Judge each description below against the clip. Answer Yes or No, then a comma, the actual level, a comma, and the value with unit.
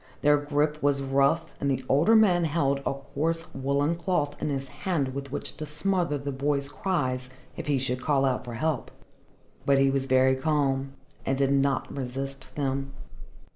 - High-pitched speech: No, medium, 140 Hz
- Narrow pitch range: Yes, narrow, 1.8 semitones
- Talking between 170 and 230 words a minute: Yes, average, 175 wpm